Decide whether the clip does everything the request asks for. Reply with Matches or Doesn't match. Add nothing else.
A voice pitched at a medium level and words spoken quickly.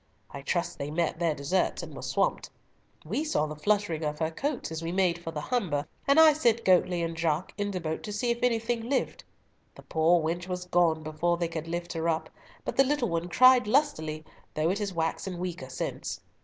Matches